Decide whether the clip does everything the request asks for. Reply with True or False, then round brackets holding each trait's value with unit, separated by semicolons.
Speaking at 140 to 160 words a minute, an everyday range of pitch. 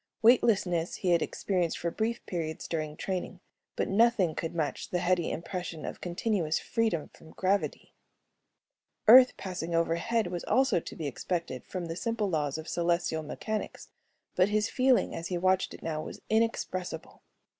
True (155 wpm; 4.4 semitones)